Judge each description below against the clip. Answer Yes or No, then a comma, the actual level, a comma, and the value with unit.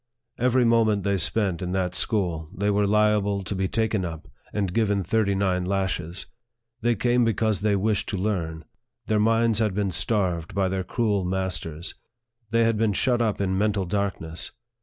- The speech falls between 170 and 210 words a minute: Yes, average, 175 wpm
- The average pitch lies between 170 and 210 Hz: No, low, 100 Hz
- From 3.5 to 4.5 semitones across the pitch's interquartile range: No, average, 2.8 semitones